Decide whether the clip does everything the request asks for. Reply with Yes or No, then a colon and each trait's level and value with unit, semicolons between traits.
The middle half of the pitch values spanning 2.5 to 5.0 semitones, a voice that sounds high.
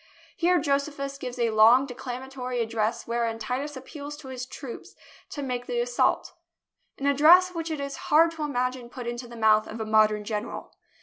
Yes: average, 3.6 semitones; very high, 255 Hz